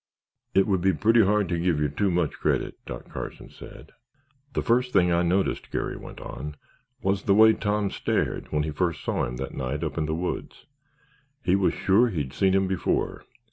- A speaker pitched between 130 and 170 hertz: No, very low, 90 Hz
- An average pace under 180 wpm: No, average, 200 wpm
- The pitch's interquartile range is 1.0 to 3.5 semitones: No, average, 4.4 semitones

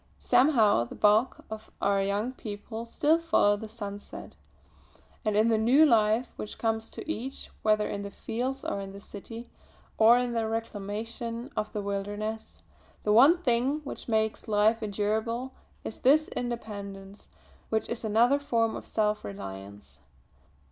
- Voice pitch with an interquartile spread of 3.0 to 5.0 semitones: No, narrow, 2.6 semitones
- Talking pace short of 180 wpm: Yes, average, 150 wpm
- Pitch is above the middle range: Yes, high, 220 Hz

